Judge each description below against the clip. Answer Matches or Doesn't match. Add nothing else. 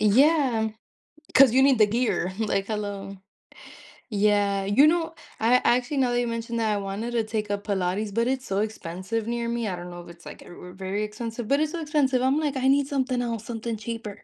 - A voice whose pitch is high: Matches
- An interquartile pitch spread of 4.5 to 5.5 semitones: Doesn't match